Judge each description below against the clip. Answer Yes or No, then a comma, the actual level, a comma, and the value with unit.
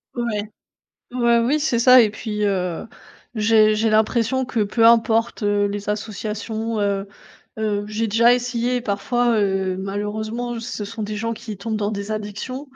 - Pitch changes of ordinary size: No, narrow, 2.3 semitones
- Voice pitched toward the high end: Yes, high, 220 Hz